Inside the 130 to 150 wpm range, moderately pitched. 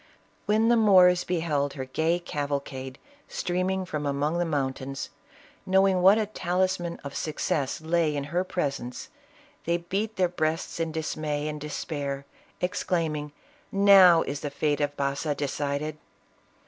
Yes: average, 140 wpm; medium, 155 Hz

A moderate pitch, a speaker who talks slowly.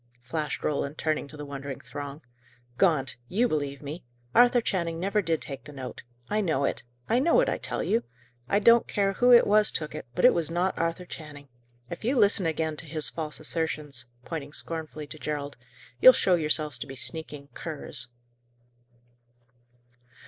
No: medium, 160 Hz; average, 180 wpm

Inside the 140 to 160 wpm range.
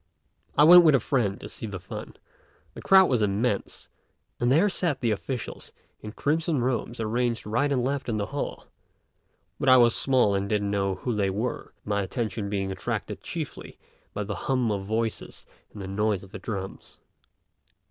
No: average, 180 wpm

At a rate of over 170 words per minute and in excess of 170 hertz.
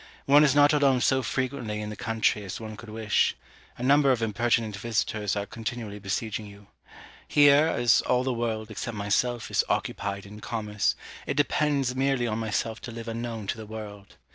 No: average, 185 wpm; low, 115 Hz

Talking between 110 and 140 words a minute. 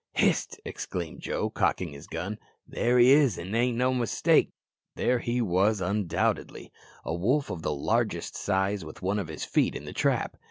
No: average, 170 wpm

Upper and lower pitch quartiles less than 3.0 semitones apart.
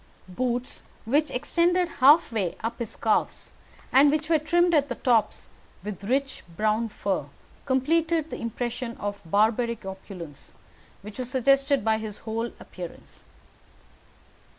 No: average, 5.0 semitones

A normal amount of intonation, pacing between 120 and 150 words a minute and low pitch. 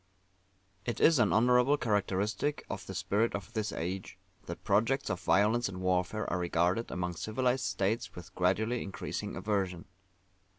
Yes: average, 4.2 semitones; average, 145 wpm; low, 100 Hz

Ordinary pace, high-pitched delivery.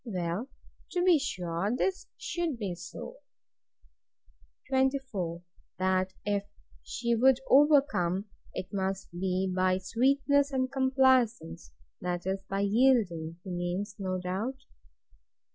No: slow, 110 wpm; high, 200 Hz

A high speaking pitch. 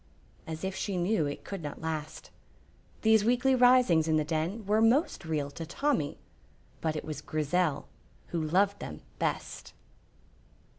No: medium, 175 Hz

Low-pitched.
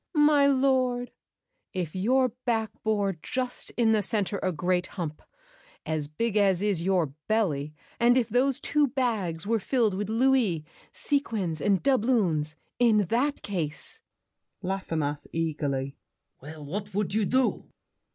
No: high, 205 Hz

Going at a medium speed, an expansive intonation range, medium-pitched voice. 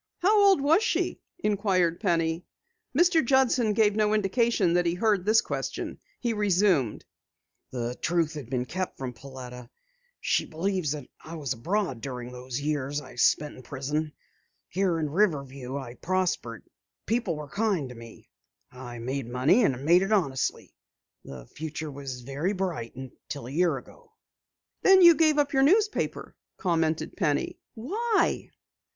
Yes: average, 150 wpm; wide, 8.0 semitones; medium, 165 Hz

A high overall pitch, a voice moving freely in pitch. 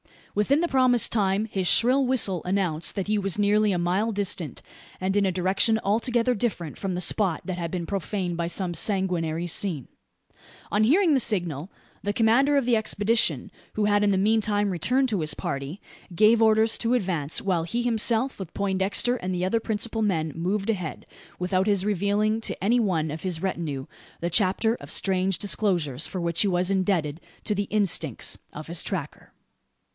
No: high, 195 Hz; average, 3.8 semitones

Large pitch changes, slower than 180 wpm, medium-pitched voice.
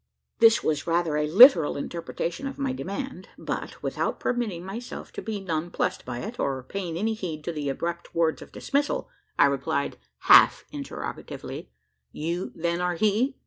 Yes: wide, 5.8 semitones; average, 160 wpm; medium, 175 Hz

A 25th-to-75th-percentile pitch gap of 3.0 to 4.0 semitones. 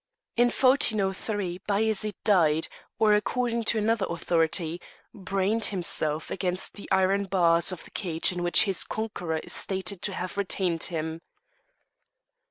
Yes: average, 3.5 semitones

